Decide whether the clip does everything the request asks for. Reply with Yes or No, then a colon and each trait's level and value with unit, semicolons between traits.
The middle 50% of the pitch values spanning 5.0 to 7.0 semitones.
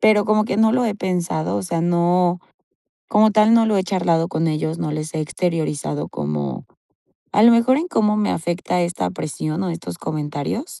Yes: wide, 5.4 semitones